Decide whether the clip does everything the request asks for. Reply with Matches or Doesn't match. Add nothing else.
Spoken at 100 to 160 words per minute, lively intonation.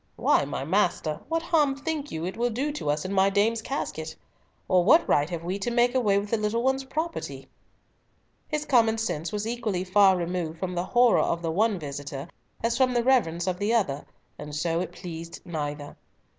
Doesn't match